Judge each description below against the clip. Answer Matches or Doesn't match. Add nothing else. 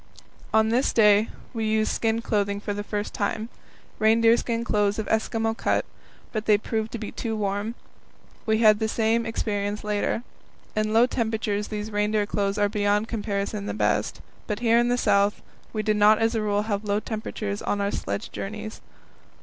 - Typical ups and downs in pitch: Doesn't match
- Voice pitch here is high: Matches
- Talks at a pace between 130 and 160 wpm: Doesn't match